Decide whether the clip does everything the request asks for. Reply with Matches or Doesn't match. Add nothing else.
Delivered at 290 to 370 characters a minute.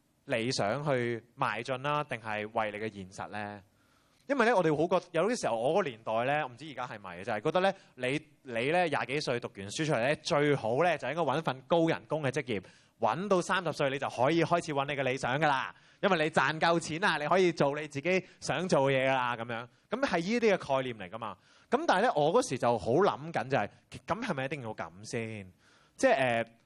Matches